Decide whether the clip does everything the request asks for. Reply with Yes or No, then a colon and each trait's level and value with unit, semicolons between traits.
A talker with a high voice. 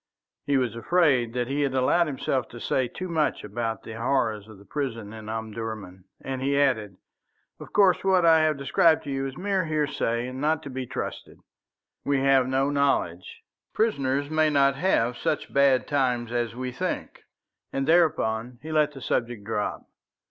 No: low, 135 Hz